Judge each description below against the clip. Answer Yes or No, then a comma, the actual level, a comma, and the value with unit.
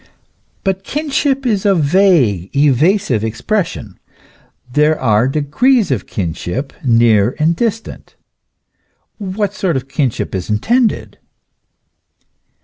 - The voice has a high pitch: No, medium, 150 Hz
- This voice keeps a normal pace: No, slow, 105 wpm